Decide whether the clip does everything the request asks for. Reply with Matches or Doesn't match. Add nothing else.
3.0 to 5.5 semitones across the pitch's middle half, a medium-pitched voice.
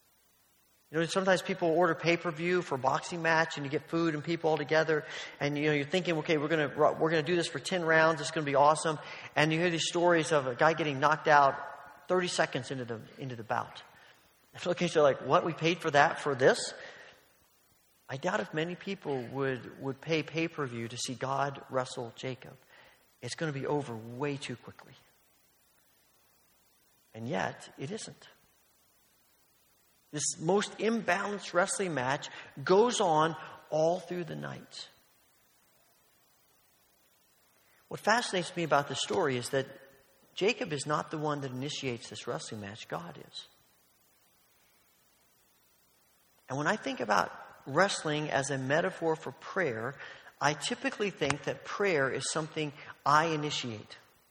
Matches